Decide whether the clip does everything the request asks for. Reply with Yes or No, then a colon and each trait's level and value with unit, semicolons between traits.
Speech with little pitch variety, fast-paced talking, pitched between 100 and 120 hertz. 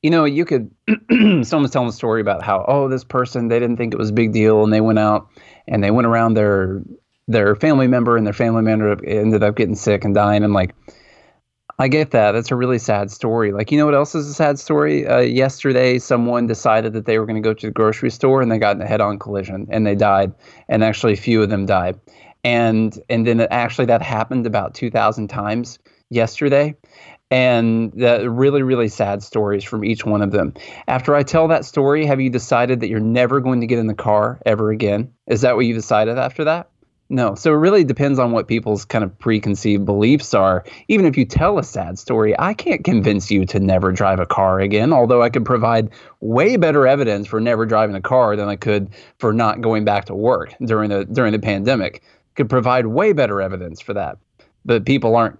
No: average, 3.3 semitones; fast, 225 wpm; low, 115 Hz